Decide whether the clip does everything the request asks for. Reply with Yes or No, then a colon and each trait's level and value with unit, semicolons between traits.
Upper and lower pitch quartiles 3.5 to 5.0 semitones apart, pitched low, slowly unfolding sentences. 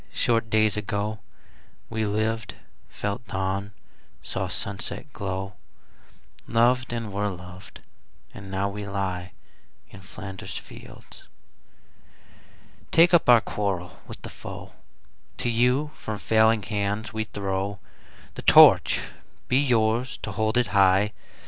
No: average, 2.7 semitones; low, 105 Hz; slow, 120 wpm